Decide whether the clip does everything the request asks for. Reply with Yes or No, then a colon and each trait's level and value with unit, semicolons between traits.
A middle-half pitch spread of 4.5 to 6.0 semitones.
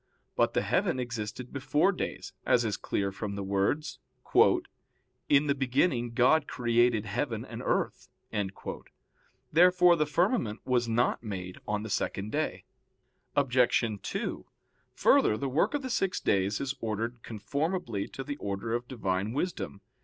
Yes: average, 5.2 semitones